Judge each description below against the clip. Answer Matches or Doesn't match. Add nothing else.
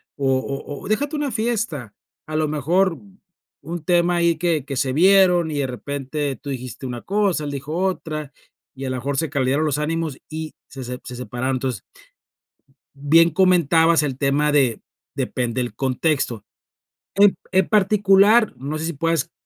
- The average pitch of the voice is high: Doesn't match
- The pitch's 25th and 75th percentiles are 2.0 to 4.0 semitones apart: Doesn't match